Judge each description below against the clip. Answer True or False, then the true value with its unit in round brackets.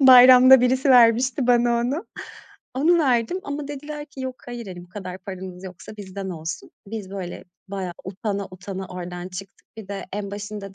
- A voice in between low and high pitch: False (210 Hz)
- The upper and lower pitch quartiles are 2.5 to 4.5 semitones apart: False (5.3 semitones)